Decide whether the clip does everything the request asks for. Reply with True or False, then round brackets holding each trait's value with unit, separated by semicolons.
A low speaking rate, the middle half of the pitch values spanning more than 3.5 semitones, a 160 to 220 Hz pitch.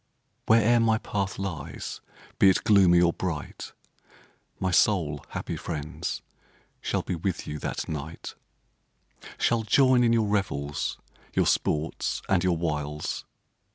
False (125 wpm; 5.4 semitones; 90 Hz)